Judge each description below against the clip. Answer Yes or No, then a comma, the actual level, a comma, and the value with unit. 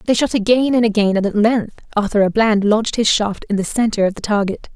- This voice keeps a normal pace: No, fast, 255 wpm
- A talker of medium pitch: No, high, 215 Hz